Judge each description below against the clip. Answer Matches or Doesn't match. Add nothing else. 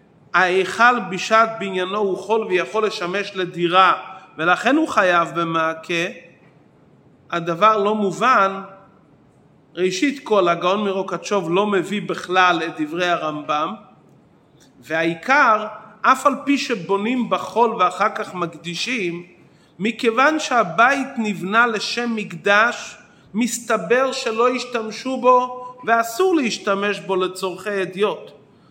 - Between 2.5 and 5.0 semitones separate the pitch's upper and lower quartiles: Matches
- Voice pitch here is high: Matches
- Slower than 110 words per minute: Matches